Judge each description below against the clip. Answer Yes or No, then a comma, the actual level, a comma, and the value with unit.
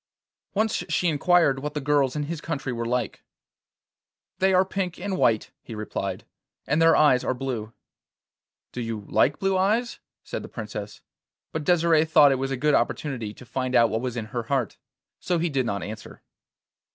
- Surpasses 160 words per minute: Yes, average, 185 wpm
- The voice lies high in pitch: No, low, 135 Hz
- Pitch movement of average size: No, wide, 5.8 semitones